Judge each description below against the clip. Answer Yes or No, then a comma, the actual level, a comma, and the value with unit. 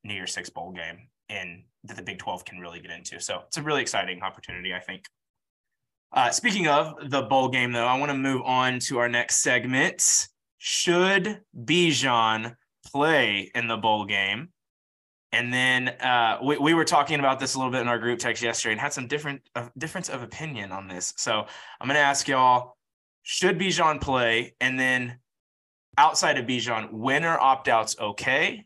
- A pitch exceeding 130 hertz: No, low, 125 Hz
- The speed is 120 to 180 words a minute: No, average, 190 wpm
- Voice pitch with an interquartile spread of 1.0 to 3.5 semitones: No, average, 3.9 semitones